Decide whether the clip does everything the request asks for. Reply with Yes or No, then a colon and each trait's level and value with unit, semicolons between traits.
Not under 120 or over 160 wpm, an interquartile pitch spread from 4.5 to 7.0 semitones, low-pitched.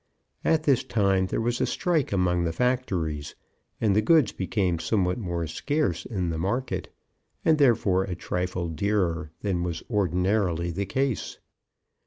Yes: average, 150 wpm; average, 5.2 semitones; very low, 95 Hz